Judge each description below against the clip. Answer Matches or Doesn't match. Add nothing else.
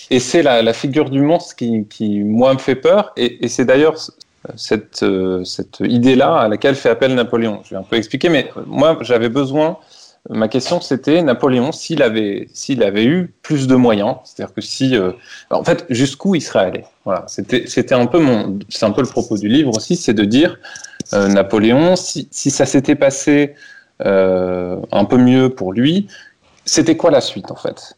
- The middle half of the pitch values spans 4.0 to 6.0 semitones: Matches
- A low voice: Matches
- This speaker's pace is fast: Doesn't match